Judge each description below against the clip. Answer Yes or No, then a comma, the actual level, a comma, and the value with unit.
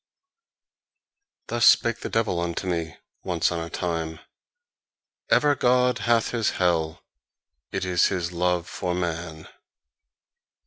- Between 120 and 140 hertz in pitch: No, very low, 90 Hz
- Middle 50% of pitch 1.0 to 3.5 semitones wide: No, average, 4.9 semitones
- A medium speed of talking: No, slow, 120 wpm